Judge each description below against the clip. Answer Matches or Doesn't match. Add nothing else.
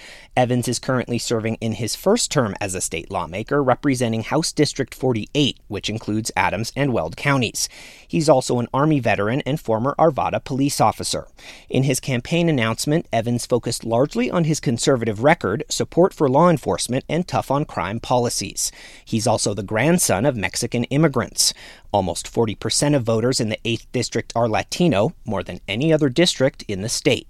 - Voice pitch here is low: Matches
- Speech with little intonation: Doesn't match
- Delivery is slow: Doesn't match